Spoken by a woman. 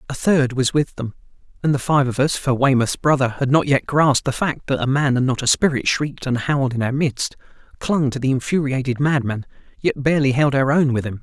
No: male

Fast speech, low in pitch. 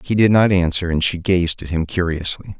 Yes: fast, 230 wpm; very low, 90 Hz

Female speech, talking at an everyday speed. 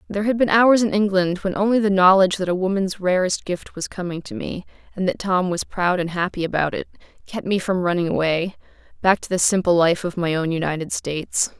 No: female; fast, 215 wpm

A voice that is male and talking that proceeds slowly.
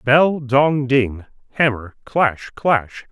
Yes: male; slow, 115 wpm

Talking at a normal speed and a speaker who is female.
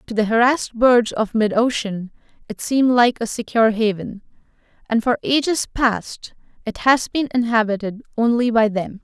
Yes: average, 160 wpm; female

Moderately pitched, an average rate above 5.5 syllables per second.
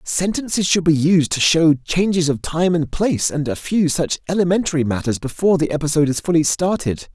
Yes: medium, 160 Hz; 5.7 syllables/s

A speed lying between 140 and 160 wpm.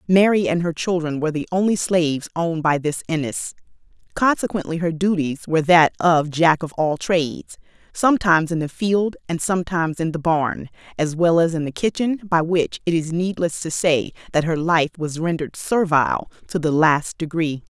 No: average, 185 wpm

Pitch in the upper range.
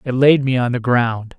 No: low, 125 Hz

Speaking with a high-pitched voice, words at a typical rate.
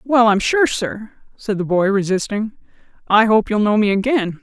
Yes: high, 215 Hz; average, 190 wpm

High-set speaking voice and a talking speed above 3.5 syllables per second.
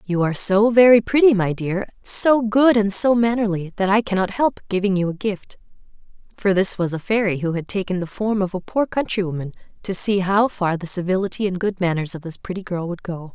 No: high, 195 Hz; 2.5 syllables/s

